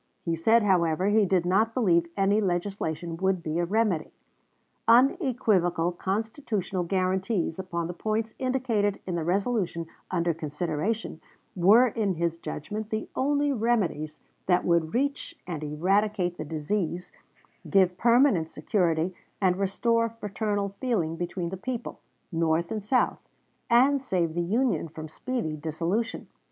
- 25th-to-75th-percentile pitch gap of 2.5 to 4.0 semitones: No, average, 4.8 semitones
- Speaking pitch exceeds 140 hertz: Yes, high, 190 Hz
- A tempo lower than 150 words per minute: Yes, slow, 135 wpm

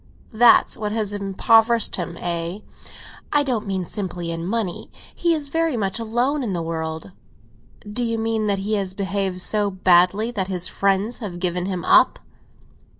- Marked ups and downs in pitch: No, average, 3.9 semitones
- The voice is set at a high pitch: Yes, high, 200 Hz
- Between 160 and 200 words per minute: Yes, average, 165 wpm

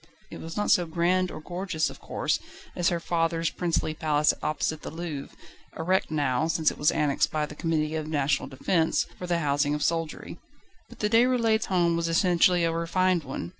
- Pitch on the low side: No, medium, 165 Hz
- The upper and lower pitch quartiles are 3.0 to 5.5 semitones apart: No, narrow, 2.6 semitones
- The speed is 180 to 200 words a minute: Yes, average, 195 wpm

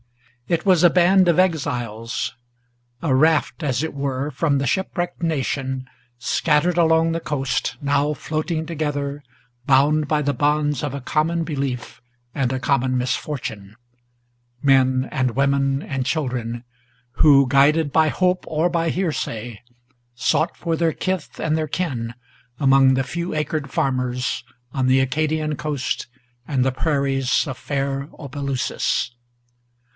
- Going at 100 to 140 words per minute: Yes, slow, 135 wpm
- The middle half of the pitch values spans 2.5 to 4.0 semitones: Yes, average, 3.2 semitones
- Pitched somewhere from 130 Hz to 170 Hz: Yes, medium, 140 Hz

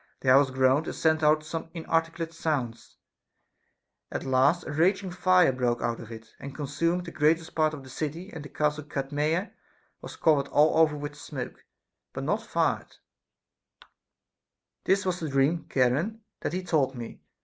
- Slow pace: No, average, 165 wpm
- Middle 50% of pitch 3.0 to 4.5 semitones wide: Yes, average, 3.4 semitones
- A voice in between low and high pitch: Yes, medium, 150 Hz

